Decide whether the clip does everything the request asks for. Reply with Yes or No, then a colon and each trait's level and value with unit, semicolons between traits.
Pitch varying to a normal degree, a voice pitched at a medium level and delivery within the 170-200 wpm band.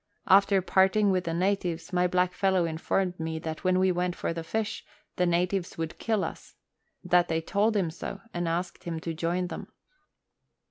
No: narrow, 2.2 semitones; medium, 180 Hz; average, 180 wpm